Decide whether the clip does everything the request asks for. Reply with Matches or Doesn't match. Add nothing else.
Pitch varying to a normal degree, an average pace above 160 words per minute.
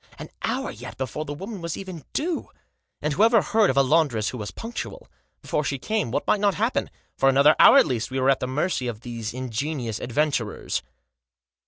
Doesn't match